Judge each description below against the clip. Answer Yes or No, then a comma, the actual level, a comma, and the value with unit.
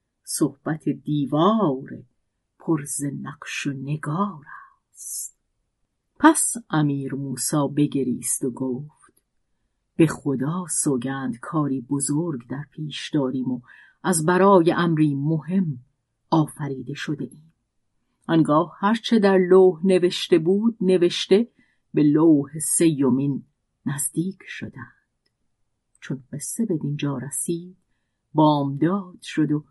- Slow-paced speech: Yes, slow, 100 wpm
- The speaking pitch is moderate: Yes, medium, 150 Hz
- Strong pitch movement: No, average, 4.1 semitones